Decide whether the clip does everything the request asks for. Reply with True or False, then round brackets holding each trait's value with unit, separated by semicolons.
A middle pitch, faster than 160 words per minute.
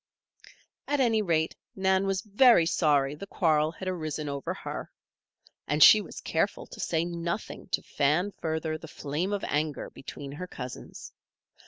False (165 Hz; 155 wpm)